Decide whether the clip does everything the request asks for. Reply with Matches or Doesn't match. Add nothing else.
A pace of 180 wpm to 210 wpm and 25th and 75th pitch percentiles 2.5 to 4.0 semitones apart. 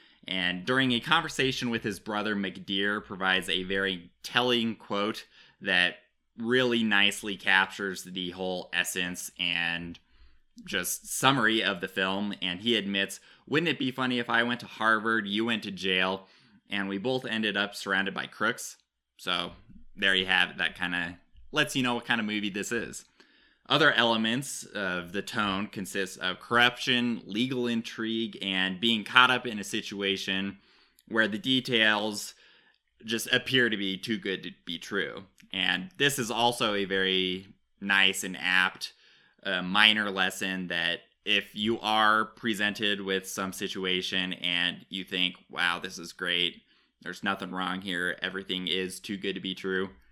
Doesn't match